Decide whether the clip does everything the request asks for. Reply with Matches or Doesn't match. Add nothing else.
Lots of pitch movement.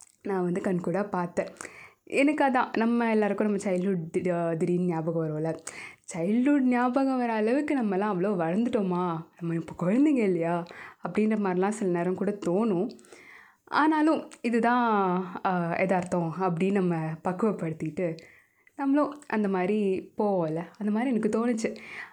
Doesn't match